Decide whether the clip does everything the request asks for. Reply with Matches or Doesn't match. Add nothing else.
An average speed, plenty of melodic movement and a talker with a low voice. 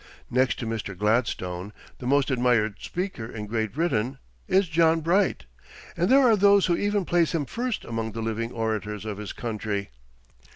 Matches